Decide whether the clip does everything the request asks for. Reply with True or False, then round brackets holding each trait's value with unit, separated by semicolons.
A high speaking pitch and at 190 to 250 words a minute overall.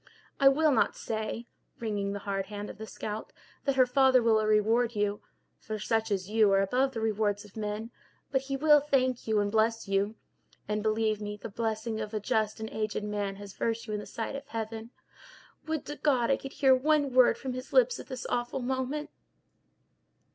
True (225 Hz; 195 wpm)